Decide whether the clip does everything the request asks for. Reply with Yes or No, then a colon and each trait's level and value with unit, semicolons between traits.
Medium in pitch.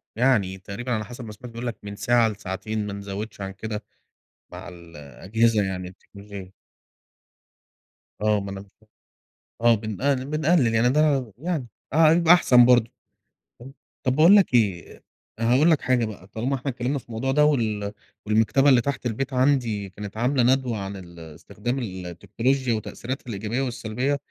No: low, 115 Hz